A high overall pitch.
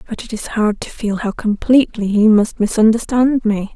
Yes: high, 220 Hz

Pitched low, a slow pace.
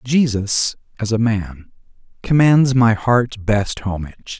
Yes: low, 115 Hz; slow, 125 wpm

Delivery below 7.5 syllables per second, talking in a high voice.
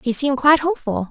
No: 7.9 syllables/s; very high, 270 Hz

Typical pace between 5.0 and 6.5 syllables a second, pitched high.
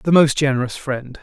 No: 5.1 syllables/s; medium, 140 Hz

